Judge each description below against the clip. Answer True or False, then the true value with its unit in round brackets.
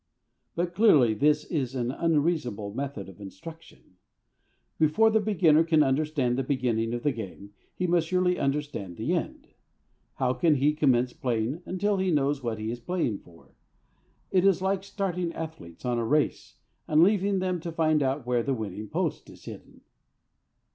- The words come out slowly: False (170 wpm)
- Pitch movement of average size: False (6.1 semitones)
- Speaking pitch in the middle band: True (150 Hz)